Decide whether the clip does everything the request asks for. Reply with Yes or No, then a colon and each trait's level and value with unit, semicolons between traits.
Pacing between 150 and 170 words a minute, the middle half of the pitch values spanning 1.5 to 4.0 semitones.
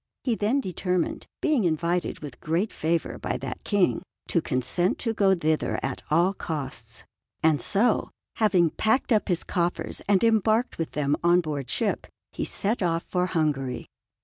No: average, 160 wpm; average, 4.7 semitones